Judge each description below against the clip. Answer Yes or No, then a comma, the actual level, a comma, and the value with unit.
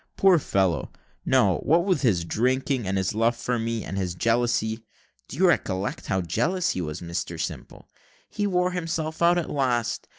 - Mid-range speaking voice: No, low, 120 Hz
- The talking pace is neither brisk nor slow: Yes, average, 175 wpm